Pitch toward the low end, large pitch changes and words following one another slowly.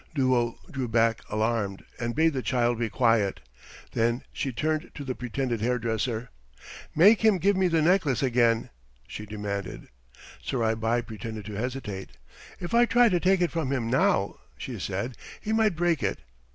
No: low, 125 Hz; wide, 6.0 semitones; average, 165 wpm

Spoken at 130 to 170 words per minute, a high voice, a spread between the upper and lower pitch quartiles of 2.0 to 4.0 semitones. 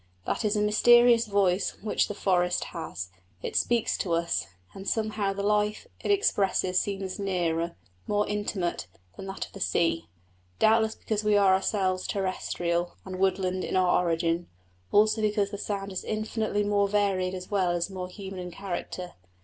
Yes: average, 165 wpm; high, 195 Hz; narrow, 2.4 semitones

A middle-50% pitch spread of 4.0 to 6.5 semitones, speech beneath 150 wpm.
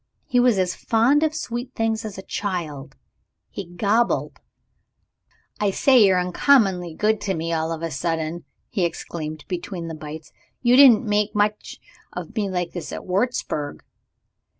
No: average, 5.1 semitones; average, 155 wpm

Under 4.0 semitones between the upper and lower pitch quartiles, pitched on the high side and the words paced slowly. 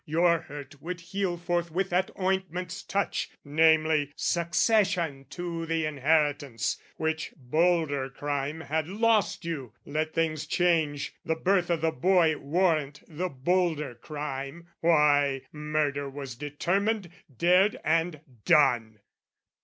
No: average, 3.4 semitones; medium, 160 Hz; slow, 115 wpm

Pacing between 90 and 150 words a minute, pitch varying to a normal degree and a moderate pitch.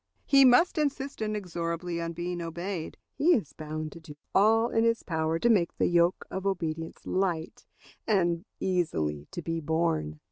No: average, 170 wpm; average, 4.4 semitones; medium, 175 Hz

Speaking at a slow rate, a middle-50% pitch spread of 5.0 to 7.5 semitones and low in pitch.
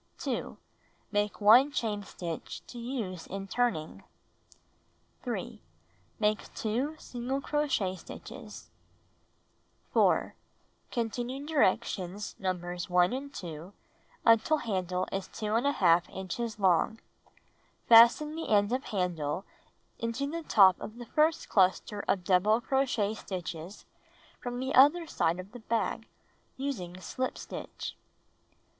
No: slow, 110 wpm; average, 5.3 semitones; high, 215 Hz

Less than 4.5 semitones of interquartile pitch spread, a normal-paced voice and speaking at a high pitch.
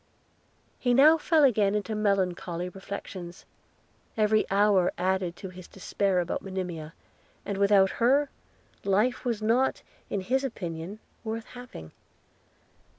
No: average, 3.8 semitones; slow, 120 wpm; high, 200 Hz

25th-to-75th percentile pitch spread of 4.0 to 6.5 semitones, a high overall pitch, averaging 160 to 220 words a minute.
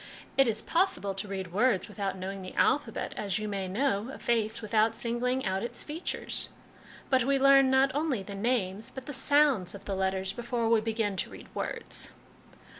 Yes: average, 5.0 semitones; high, 225 Hz; average, 190 wpm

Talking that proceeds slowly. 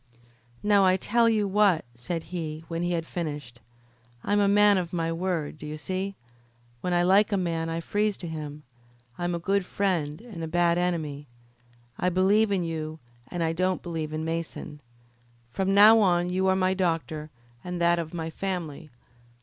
No: average, 180 wpm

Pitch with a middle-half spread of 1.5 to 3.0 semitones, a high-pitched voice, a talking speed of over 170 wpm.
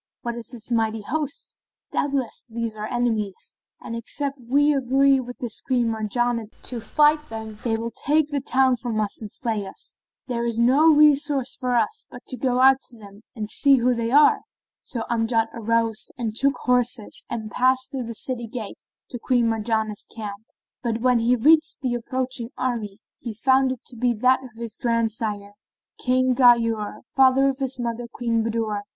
Yes: narrow, 2.6 semitones; high, 240 Hz; average, 180 wpm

